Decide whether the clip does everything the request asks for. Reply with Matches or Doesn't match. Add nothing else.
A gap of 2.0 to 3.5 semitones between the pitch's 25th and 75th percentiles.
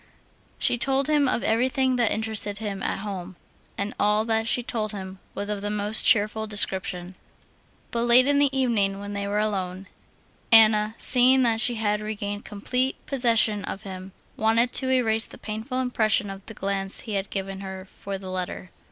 Matches